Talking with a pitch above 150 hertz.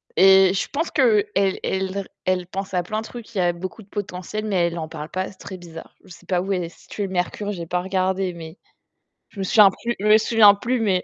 Yes: high, 190 Hz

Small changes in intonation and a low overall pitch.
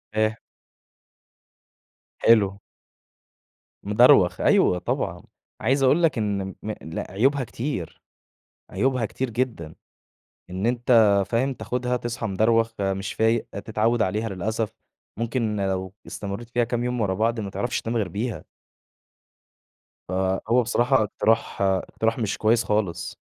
No: average, 3.4 semitones; low, 110 Hz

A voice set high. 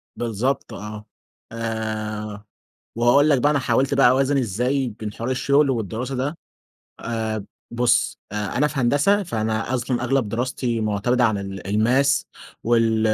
No: low, 120 Hz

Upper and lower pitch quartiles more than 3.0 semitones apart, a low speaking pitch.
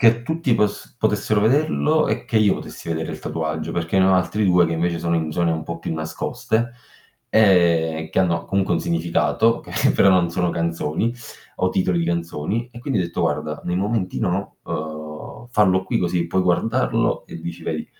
Yes: average, 4.3 semitones; very low, 90 Hz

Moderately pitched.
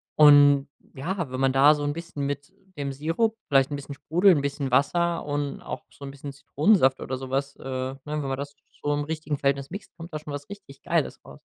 Yes: medium, 145 Hz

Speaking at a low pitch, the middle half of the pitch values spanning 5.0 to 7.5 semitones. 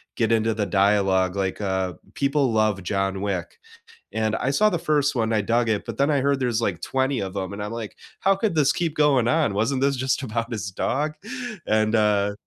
Yes: low, 115 Hz; average, 5.3 semitones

